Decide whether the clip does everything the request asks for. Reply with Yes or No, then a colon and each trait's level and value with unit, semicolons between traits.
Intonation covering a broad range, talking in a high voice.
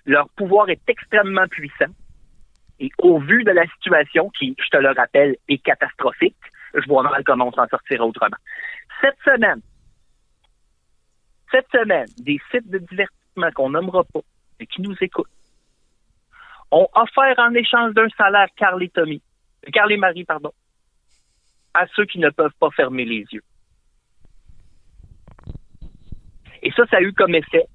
Yes: wide, 6.8 semitones; high, 200 Hz